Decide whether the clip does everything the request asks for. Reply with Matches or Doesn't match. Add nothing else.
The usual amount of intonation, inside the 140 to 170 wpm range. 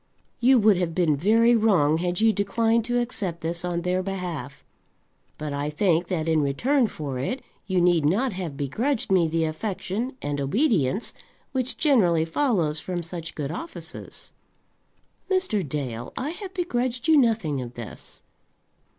Doesn't match